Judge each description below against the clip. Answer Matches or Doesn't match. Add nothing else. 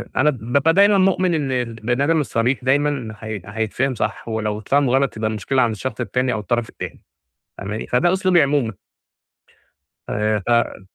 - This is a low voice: Matches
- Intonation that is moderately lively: Matches